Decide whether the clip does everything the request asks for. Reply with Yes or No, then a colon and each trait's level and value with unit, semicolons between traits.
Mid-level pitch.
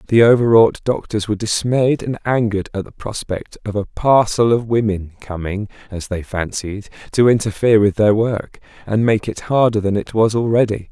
No: low, 110 Hz